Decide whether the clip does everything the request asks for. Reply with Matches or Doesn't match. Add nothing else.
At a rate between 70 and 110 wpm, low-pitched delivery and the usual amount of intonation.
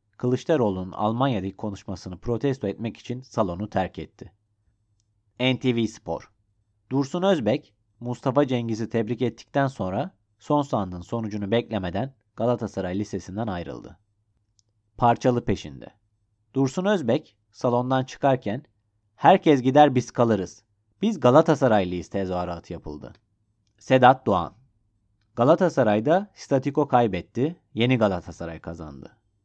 Matches